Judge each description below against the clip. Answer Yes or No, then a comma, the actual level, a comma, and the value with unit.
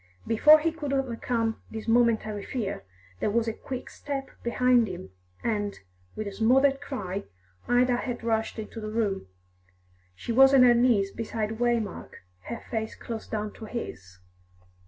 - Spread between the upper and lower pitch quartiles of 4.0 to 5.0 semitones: No, average, 2.8 semitones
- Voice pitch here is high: Yes, high, 230 Hz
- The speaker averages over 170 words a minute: No, average, 155 wpm